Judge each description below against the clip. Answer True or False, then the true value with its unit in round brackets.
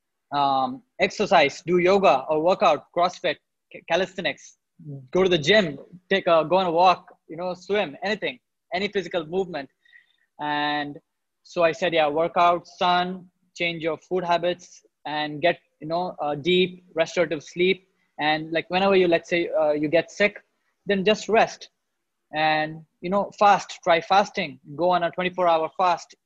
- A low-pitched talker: False (175 Hz)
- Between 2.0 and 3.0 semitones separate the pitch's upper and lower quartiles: True (2.5 semitones)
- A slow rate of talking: False (160 wpm)